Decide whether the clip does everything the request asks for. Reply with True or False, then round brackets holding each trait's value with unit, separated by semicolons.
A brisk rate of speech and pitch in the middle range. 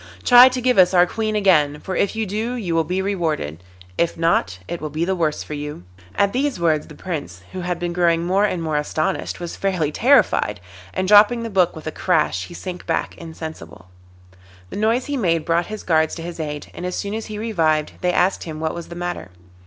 True (225 wpm; 175 Hz)